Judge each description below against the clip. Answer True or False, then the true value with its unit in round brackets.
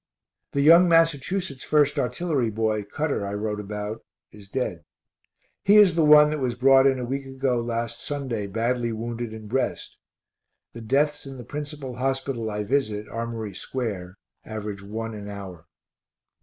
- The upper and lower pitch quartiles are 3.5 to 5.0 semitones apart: True (4.5 semitones)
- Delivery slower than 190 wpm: True (155 wpm)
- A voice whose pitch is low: True (120 Hz)